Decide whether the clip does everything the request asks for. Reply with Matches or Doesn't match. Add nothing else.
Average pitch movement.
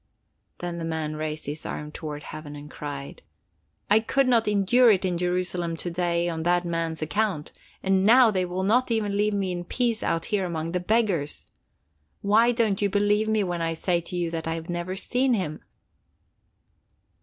Matches